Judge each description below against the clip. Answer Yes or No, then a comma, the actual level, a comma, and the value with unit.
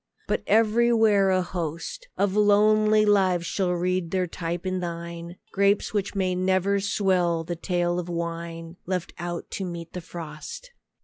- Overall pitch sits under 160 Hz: No, medium, 185 Hz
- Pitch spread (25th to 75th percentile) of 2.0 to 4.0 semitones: Yes, average, 2.8 semitones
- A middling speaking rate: Yes, average, 150 wpm